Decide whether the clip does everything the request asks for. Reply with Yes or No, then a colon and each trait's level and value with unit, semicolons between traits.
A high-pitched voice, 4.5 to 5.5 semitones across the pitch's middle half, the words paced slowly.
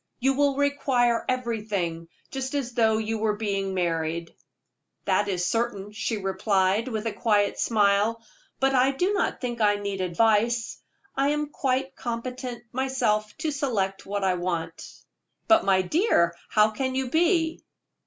No: high, 225 Hz; average, 4.8 semitones; average, 155 wpm